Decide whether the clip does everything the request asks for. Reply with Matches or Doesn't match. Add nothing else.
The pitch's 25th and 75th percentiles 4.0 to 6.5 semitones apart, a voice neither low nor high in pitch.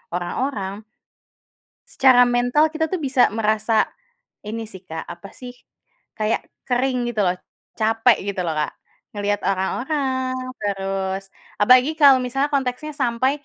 Doesn't match